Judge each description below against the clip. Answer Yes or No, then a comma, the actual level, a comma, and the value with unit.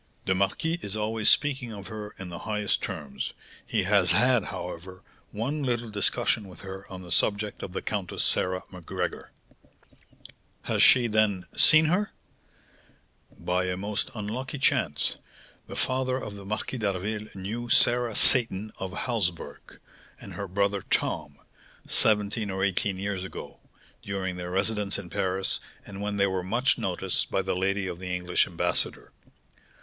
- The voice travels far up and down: No, average, 2.8 semitones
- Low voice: Yes, low, 100 Hz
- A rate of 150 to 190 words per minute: Yes, average, 155 wpm